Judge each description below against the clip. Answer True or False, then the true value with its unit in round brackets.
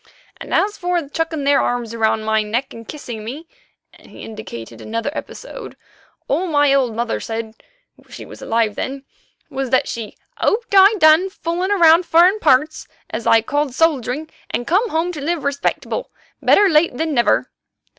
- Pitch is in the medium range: False (285 Hz)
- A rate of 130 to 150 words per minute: False (160 wpm)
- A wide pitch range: True (6.5 semitones)